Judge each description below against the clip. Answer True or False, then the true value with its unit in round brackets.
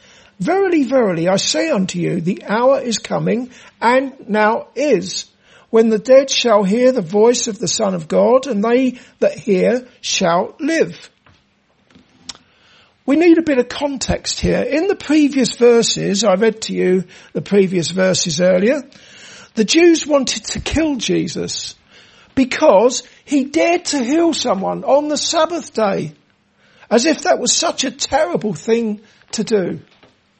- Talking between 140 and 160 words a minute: True (150 wpm)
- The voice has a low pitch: False (240 Hz)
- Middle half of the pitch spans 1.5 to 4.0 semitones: False (5.4 semitones)